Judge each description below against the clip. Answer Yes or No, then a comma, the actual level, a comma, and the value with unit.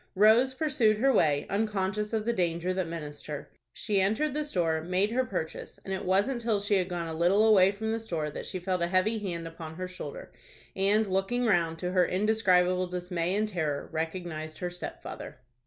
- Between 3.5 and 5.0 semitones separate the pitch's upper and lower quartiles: Yes, average, 3.9 semitones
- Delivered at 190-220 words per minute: Yes, average, 200 wpm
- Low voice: No, medium, 185 Hz